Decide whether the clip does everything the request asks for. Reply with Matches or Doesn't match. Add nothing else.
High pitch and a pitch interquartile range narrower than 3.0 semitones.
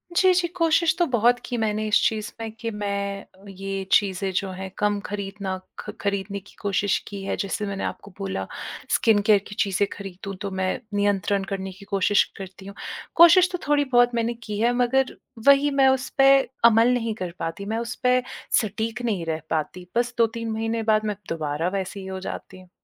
Doesn't match